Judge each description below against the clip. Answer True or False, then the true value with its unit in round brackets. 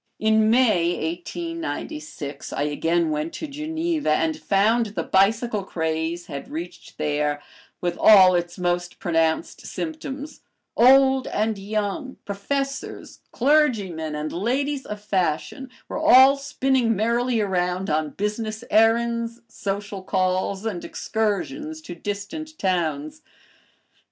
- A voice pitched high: True (205 Hz)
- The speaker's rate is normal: False (115 wpm)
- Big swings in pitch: True (6.5 semitones)